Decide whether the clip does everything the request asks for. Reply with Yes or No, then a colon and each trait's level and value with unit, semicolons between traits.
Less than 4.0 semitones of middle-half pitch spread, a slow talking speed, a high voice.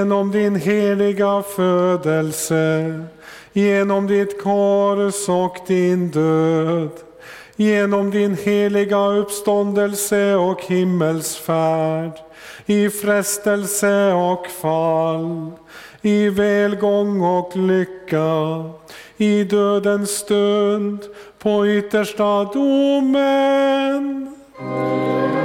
Yes: average, 3.5 semitones; slow, 70 wpm; high, 200 Hz